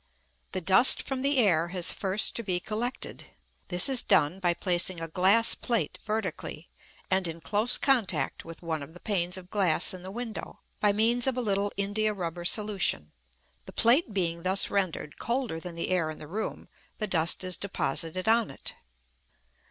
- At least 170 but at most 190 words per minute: Yes, average, 180 wpm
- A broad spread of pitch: No, average, 4.1 semitones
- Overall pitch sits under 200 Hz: Yes, high, 190 Hz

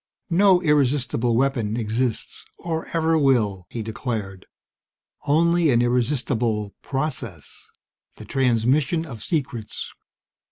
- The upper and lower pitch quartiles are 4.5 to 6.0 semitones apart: Yes, average, 4.9 semitones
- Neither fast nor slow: No, slow, 95 wpm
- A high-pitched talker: No, low, 125 Hz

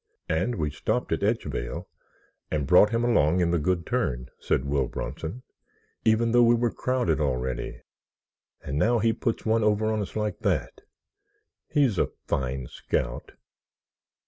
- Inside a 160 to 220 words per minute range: No, average, 150 wpm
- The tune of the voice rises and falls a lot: Yes, wide, 7.8 semitones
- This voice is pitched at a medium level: No, very low, 95 Hz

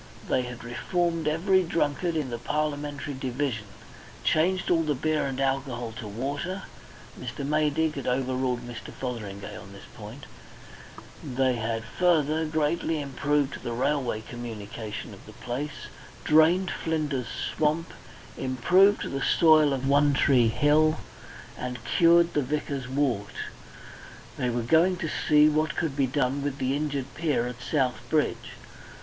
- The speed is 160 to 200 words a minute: No, average, 145 wpm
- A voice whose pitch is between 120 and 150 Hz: Yes, medium, 140 Hz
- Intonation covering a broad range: No, average, 3.8 semitones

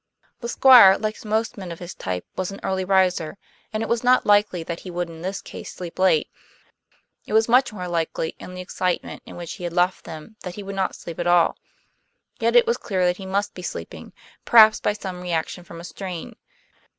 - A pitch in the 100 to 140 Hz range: No, medium, 185 Hz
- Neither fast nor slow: No, fast, 220 wpm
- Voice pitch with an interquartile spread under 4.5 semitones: Yes, average, 3.1 semitones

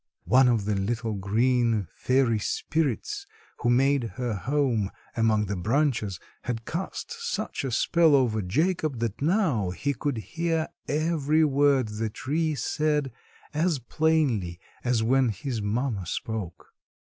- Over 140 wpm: No, slow, 135 wpm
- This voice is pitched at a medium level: No, low, 125 Hz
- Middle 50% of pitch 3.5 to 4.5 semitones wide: No, wide, 5.6 semitones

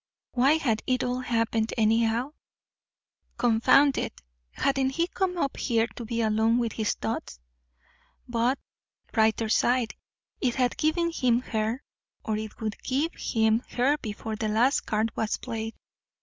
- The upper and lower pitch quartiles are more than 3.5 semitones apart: No, average, 3.0 semitones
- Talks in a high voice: Yes, high, 235 Hz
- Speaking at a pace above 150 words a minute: No, average, 145 wpm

